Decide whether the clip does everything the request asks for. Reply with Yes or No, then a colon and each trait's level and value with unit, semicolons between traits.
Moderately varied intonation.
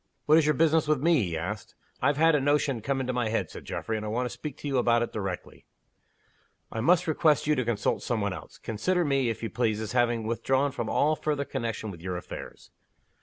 Yes: average, 5.0 semitones